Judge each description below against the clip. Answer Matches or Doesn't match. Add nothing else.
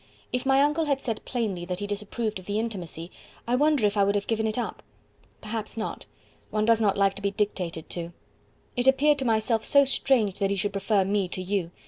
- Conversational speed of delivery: Doesn't match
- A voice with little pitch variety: Doesn't match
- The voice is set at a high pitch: Matches